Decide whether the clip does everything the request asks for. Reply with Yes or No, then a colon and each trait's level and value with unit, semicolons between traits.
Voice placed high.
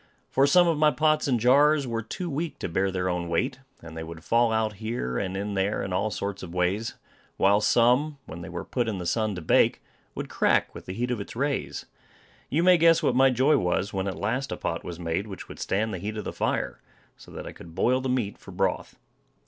No: low, 110 Hz